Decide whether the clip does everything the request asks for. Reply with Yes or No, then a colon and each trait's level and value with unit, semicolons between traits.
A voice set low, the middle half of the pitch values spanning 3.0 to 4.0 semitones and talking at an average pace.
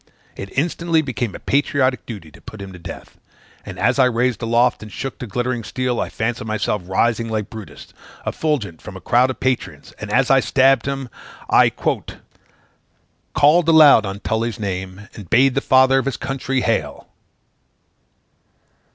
Yes: low, 120 Hz; average, 3.7 semitones; average, 165 wpm